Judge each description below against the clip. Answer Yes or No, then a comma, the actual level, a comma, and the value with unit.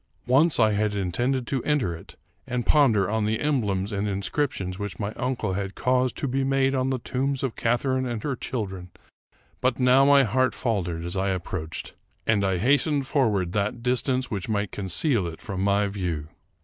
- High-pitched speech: No, low, 110 Hz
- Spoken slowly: No, average, 180 wpm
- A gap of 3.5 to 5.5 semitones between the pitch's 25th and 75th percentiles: Yes, average, 5.1 semitones